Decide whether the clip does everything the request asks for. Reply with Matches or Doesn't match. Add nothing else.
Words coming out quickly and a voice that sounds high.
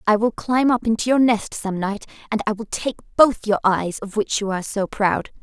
Matches